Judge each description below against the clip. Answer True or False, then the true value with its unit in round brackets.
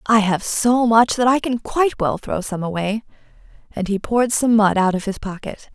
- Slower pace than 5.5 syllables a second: True (5.0 syllables/s)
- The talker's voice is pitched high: True (220 Hz)